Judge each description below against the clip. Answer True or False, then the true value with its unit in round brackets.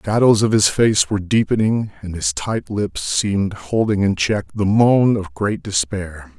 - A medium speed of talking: True (190 wpm)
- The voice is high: False (100 Hz)